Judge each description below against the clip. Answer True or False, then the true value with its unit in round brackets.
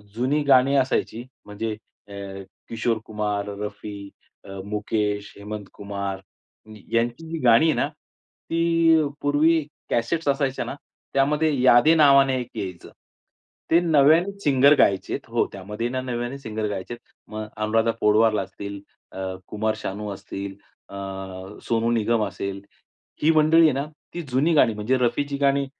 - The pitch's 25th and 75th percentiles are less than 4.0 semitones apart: False (5.0 semitones)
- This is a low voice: True (115 Hz)